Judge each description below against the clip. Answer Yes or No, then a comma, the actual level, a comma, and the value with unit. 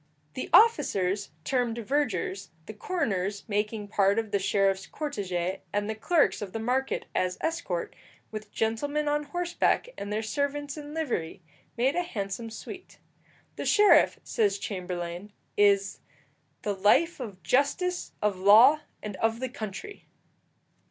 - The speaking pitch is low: No, high, 220 Hz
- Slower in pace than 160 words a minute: Yes, average, 140 wpm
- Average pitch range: No, wide, 6.6 semitones